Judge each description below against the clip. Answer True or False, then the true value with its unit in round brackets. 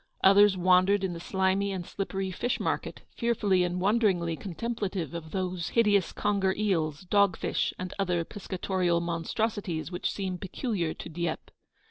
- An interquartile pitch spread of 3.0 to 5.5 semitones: False (2.6 semitones)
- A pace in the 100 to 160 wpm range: True (145 wpm)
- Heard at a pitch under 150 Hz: False (185 Hz)